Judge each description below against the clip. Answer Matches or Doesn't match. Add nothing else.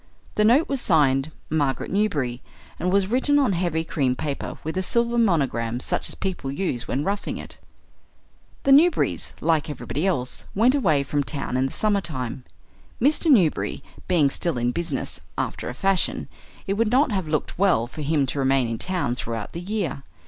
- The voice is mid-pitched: Matches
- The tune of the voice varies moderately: Doesn't match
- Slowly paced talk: Doesn't match